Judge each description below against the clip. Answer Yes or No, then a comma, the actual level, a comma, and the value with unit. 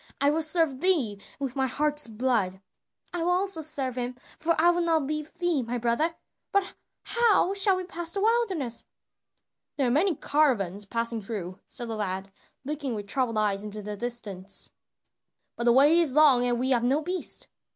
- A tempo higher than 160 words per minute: Yes, average, 180 wpm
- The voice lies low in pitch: No, very high, 270 Hz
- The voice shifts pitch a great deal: Yes, wide, 6.2 semitones